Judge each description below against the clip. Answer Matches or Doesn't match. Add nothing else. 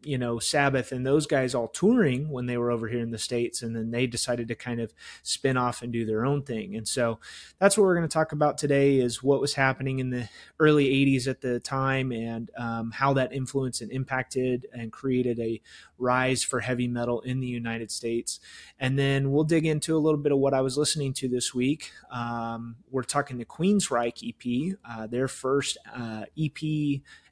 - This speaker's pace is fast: Matches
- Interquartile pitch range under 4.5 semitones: Matches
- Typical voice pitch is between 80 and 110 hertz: Doesn't match